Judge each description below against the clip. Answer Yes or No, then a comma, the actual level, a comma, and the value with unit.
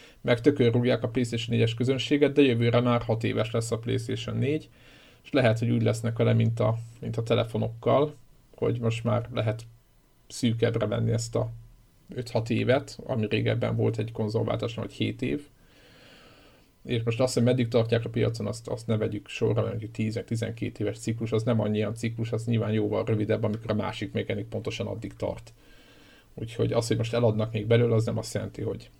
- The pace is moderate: No, fast, 185 wpm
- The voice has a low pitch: Yes, low, 115 Hz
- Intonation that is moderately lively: No, narrow, 1.6 semitones